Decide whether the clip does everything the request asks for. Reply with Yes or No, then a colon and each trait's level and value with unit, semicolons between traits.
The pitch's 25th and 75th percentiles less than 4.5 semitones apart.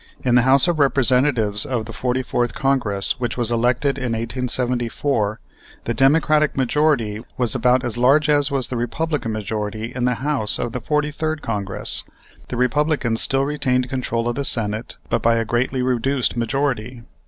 Yes: average, 3.0 semitones